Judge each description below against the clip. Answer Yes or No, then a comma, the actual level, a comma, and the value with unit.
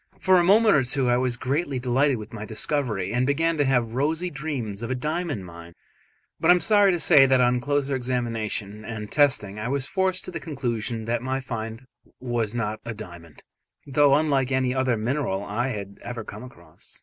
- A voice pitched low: Yes, low, 125 Hz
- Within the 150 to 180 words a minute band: No, average, 200 wpm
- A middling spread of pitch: Yes, average, 4.6 semitones